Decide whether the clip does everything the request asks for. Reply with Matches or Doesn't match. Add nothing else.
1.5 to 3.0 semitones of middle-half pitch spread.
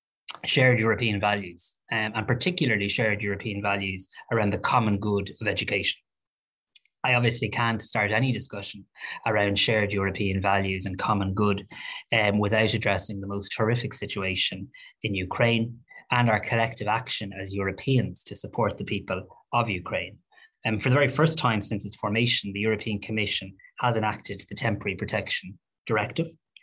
Matches